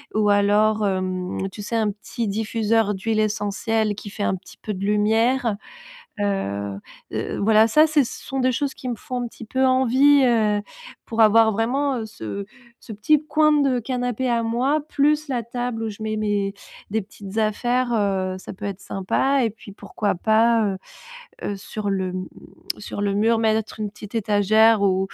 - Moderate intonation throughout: Yes, average, 3.1 semitones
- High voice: Yes, high, 220 Hz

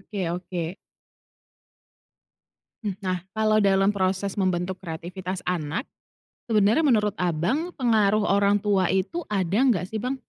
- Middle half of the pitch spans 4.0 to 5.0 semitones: No, average, 2.7 semitones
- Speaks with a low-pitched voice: No, high, 200 Hz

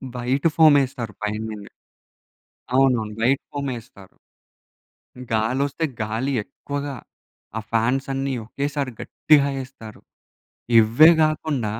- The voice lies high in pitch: No, low, 130 Hz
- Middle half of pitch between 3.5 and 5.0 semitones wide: Yes, average, 4.1 semitones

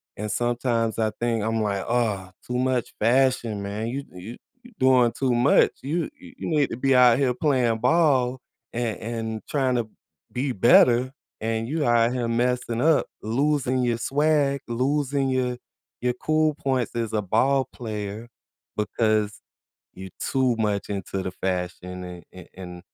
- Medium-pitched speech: No, low, 120 Hz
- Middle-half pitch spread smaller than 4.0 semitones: Yes, average, 3.3 semitones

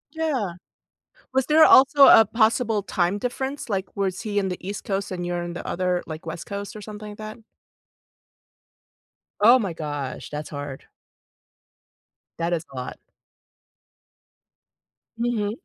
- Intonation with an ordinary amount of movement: Yes, average, 4.6 semitones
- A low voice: No, high, 200 Hz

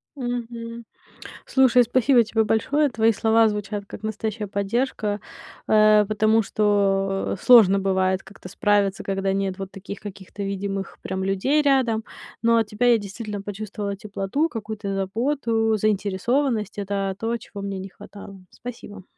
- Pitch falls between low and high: No, high, 210 Hz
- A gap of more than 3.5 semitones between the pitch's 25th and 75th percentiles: No, average, 2.8 semitones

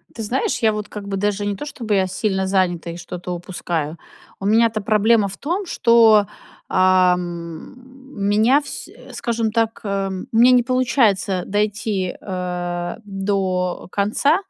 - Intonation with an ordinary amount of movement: Yes, average, 3.4 semitones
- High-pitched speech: Yes, high, 200 Hz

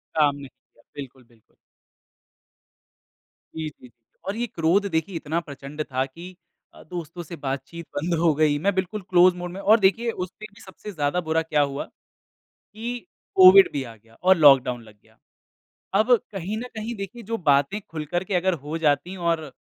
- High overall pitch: No, medium, 170 Hz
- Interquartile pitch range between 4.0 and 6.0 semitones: Yes, average, 5.2 semitones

